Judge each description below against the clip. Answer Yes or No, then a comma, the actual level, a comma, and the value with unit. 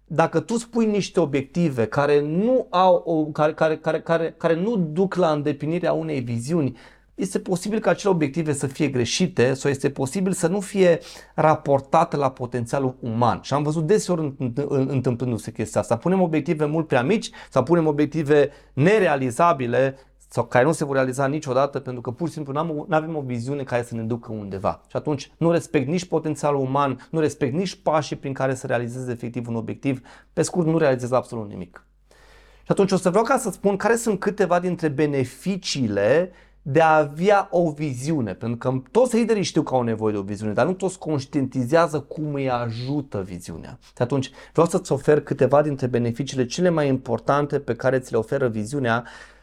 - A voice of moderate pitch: Yes, medium, 145 Hz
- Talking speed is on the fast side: Yes, fast, 185 wpm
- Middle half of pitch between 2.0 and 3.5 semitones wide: No, average, 4.8 semitones